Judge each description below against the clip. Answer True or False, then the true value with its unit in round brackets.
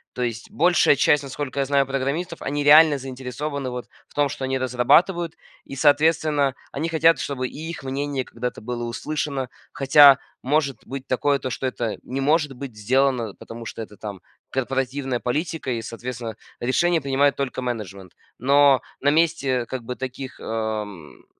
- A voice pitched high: False (135 Hz)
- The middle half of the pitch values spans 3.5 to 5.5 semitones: False (2.8 semitones)